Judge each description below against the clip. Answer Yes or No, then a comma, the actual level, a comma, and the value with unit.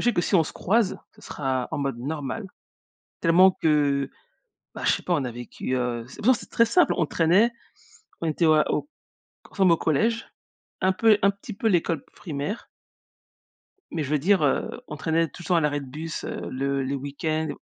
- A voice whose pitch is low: No, medium, 160 Hz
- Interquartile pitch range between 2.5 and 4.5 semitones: No, average, 5.1 semitones